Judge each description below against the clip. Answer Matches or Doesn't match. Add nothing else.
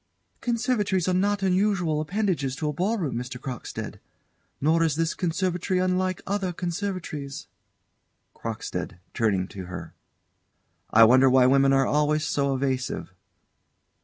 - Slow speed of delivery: Matches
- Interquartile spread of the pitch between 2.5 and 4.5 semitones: Doesn't match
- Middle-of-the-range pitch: Matches